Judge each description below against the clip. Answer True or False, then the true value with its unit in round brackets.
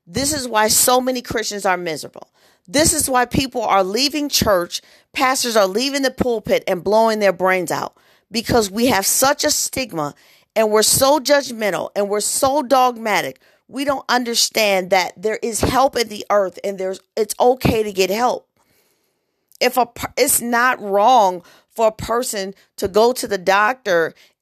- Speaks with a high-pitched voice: True (225 Hz)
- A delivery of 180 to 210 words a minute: False (170 wpm)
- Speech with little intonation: False (4.5 semitones)